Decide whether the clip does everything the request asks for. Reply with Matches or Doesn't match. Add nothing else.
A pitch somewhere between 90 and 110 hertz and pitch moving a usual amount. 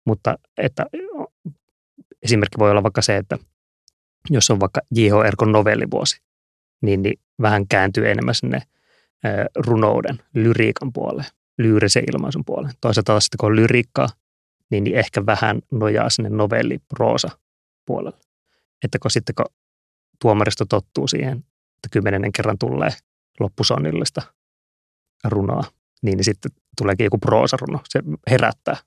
Matches